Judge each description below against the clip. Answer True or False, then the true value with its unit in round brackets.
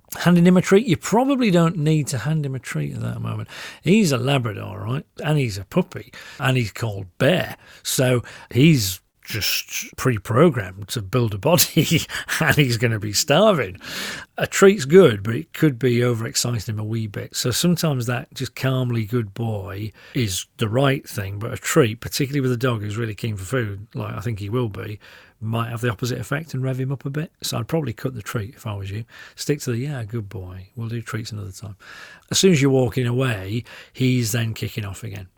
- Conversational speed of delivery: False (215 wpm)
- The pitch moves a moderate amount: True (4.3 semitones)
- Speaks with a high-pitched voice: False (125 Hz)